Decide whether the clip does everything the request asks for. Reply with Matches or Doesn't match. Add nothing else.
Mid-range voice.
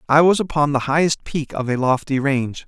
Matches